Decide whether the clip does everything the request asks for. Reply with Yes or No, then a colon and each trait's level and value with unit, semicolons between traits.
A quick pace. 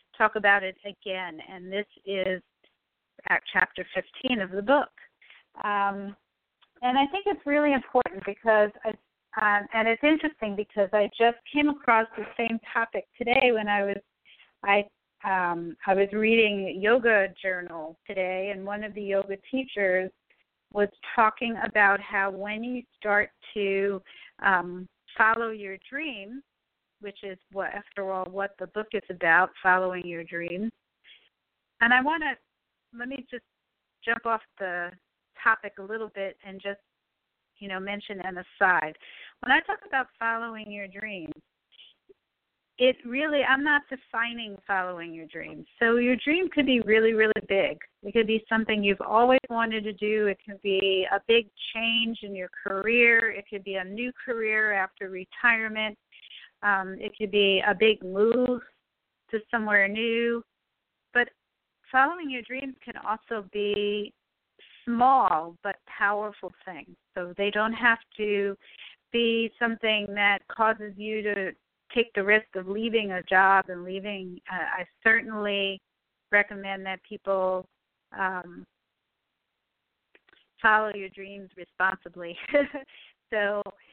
No: average, 145 wpm